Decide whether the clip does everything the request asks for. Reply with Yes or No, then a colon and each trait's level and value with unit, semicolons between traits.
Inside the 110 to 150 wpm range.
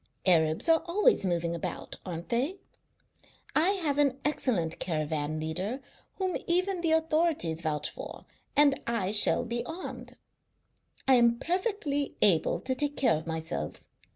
Yes: average, 140 wpm